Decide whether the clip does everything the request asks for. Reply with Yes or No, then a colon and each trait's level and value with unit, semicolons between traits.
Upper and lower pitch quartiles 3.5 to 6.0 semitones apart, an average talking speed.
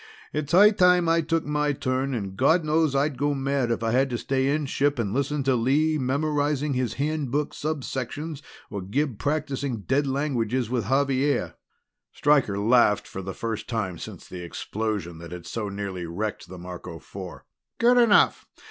Yes: average, 5.2 semitones; average, 175 wpm